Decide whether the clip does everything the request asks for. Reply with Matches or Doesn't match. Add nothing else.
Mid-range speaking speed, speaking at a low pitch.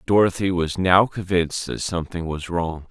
Matches